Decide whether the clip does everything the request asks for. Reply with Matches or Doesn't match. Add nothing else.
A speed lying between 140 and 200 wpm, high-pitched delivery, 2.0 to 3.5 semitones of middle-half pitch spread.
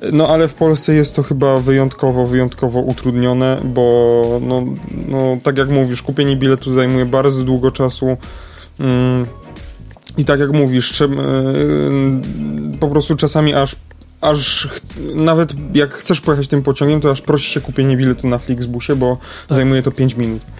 Doesn't match